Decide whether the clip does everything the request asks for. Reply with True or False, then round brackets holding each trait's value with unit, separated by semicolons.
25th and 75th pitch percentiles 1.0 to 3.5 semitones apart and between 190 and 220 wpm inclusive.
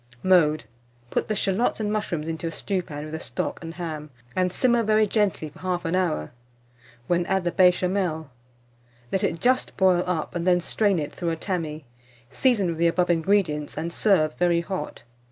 False (3.0 semitones; 180 wpm)